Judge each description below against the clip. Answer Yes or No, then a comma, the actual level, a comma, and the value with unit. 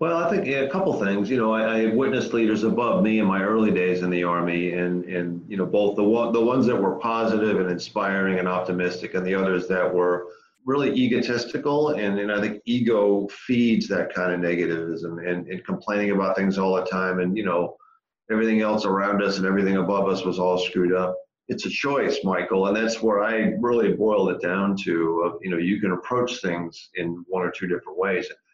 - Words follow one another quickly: Yes, fast, 220 wpm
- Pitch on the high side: No, low, 100 Hz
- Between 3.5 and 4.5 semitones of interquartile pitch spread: Yes, average, 4.1 semitones